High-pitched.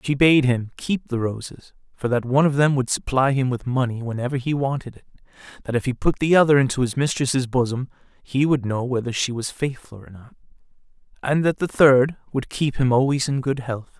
No: low, 130 Hz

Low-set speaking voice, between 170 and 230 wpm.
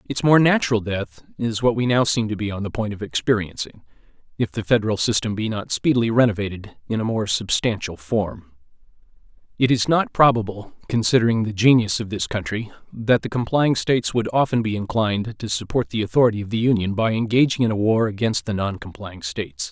Yes: low, 110 Hz; average, 195 wpm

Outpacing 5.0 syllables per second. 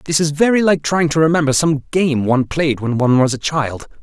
Yes: 5.7 syllables/s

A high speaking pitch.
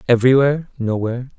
No: low, 125 Hz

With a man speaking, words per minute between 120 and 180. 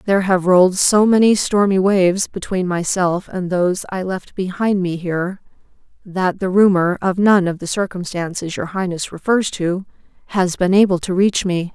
No: female; average, 175 wpm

